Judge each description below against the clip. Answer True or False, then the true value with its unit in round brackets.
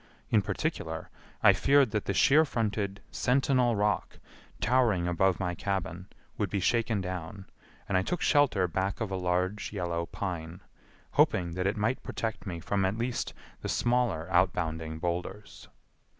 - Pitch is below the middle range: True (95 Hz)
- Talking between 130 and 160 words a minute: True (150 wpm)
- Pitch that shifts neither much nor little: True (3.8 semitones)